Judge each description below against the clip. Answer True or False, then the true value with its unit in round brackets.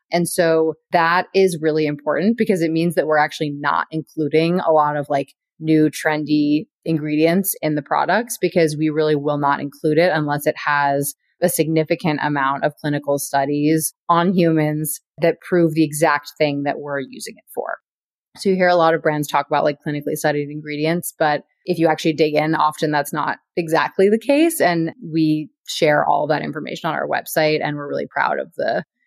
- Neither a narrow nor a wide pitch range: False (2.0 semitones)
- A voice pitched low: False (155 Hz)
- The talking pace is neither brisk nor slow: True (190 wpm)